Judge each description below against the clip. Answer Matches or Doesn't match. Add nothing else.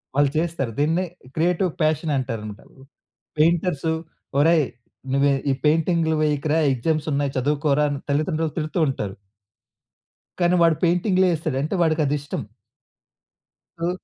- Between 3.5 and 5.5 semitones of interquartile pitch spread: Doesn't match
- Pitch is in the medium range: Matches